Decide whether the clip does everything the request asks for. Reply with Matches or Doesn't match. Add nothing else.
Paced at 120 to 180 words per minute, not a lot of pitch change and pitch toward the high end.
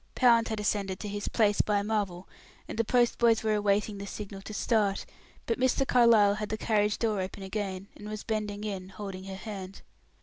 Doesn't match